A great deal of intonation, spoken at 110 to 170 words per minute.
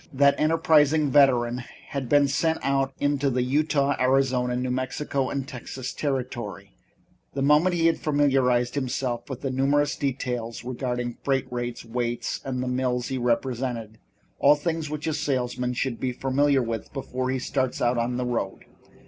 No: narrow, 2.5 semitones; average, 160 wpm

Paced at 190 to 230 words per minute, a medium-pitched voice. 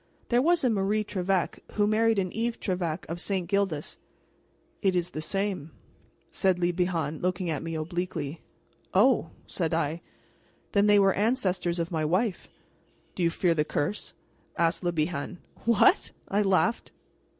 No: average, 160 wpm; medium, 180 Hz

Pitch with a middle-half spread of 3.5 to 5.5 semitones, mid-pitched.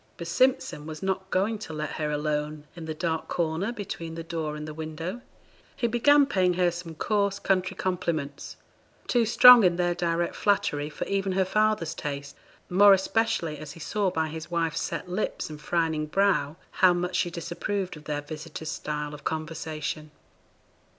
Yes: average, 3.8 semitones; medium, 170 Hz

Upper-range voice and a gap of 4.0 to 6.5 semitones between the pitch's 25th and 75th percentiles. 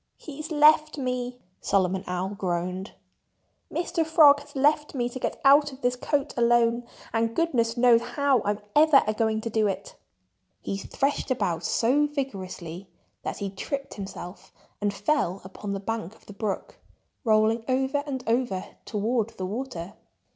Yes: high, 235 Hz; wide, 5.6 semitones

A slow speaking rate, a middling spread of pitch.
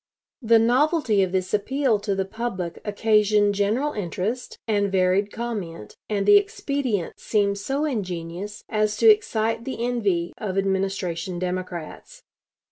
Yes: slow, 130 wpm; average, 3.8 semitones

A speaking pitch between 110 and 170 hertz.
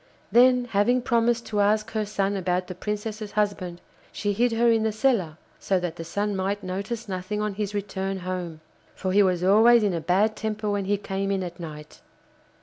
No: high, 205 Hz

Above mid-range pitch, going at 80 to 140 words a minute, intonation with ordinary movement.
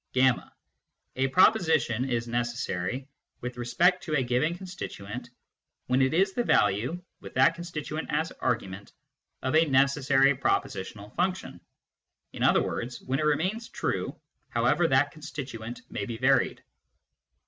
No: low, 135 Hz; slow, 135 wpm; average, 5.0 semitones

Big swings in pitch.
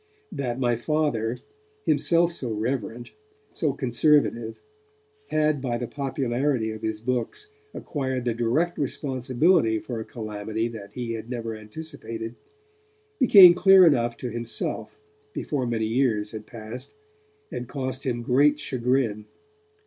No: average, 4.1 semitones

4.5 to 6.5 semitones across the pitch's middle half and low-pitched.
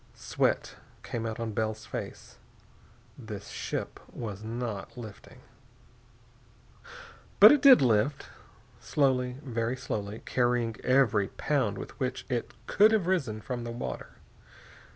No: average, 3.0 semitones; low, 120 Hz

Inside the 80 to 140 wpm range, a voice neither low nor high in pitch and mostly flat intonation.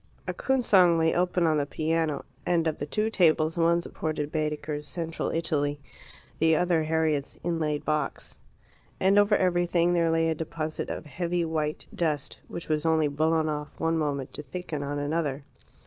No: average, 170 wpm; medium, 160 Hz; narrow, 2.1 semitones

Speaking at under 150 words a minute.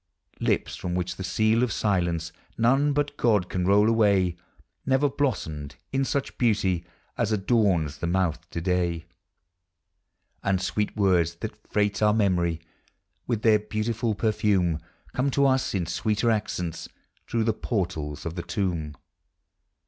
Yes: average, 140 wpm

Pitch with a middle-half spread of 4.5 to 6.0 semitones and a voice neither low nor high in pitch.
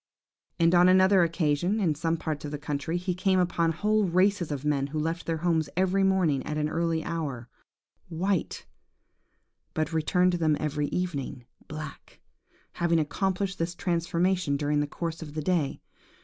No: average, 3.1 semitones; medium, 165 Hz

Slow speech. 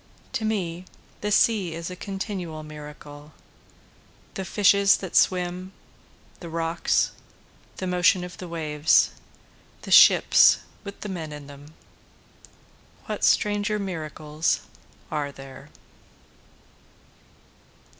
Yes: slow, 105 wpm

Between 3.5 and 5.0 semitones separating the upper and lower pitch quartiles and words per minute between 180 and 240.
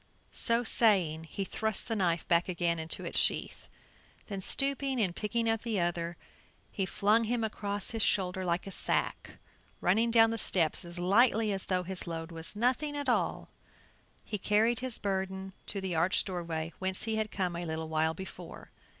Yes: average, 4.5 semitones; average, 185 wpm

